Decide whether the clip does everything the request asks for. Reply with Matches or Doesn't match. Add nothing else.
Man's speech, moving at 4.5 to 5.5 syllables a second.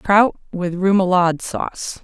Doesn't match